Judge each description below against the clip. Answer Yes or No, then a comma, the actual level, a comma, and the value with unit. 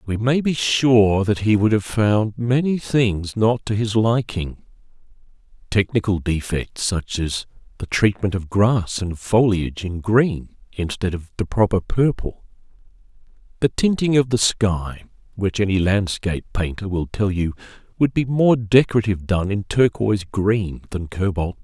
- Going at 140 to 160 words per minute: Yes, average, 155 wpm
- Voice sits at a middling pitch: No, low, 105 Hz